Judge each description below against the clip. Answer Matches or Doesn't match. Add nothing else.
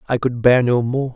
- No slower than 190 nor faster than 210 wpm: Doesn't match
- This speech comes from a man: Matches